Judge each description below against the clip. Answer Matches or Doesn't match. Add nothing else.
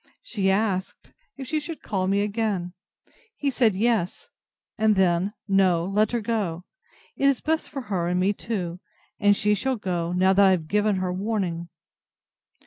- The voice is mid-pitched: Doesn't match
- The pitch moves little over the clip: Doesn't match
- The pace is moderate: Matches